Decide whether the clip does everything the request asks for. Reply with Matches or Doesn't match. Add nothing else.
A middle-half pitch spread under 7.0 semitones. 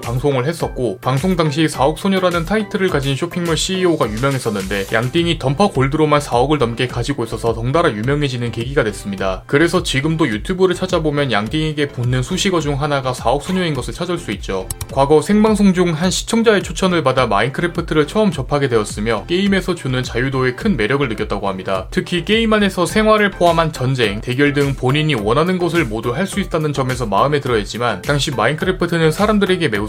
Matches